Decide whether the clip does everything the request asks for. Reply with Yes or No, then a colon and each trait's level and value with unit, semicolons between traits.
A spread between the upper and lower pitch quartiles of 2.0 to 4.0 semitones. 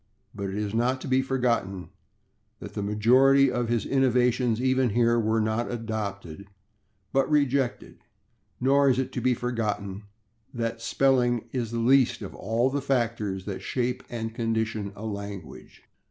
Yes: average, 3.3 semitones